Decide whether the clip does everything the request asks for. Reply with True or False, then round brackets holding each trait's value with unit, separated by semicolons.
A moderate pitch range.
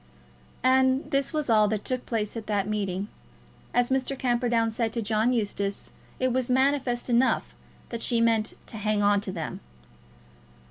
True (3.3 semitones)